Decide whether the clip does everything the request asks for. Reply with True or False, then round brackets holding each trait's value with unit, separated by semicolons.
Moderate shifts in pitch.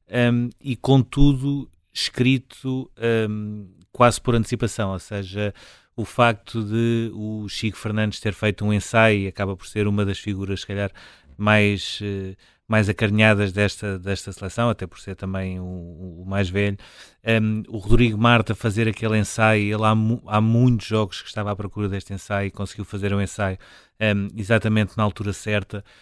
False (2.2 semitones)